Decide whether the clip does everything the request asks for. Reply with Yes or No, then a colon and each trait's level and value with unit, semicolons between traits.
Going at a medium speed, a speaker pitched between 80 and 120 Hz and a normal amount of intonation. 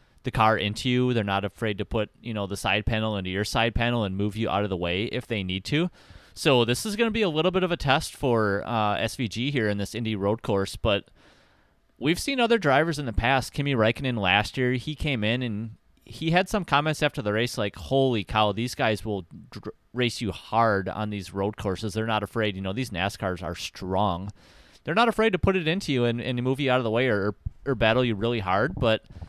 No: fast, 245 wpm; low, 115 Hz; average, 4.2 semitones